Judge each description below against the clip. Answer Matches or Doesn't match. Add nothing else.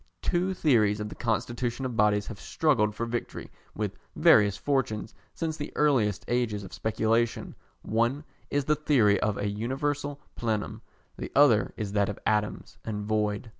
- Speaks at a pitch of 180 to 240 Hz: Doesn't match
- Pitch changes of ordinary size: Matches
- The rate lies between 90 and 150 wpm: Doesn't match